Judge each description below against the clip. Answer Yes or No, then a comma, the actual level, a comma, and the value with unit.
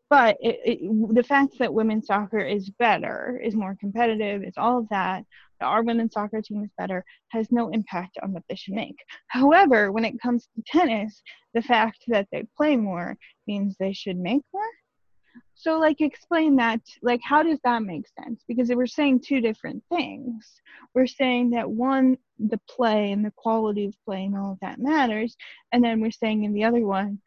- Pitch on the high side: Yes, high, 230 Hz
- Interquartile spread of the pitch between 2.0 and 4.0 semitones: Yes, average, 3.4 semitones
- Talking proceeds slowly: No, average, 195 wpm